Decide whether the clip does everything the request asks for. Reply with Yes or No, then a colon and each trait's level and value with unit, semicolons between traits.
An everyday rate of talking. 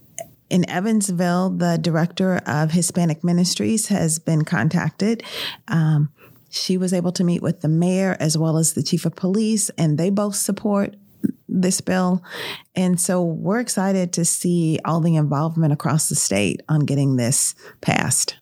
Yes: average, 155 wpm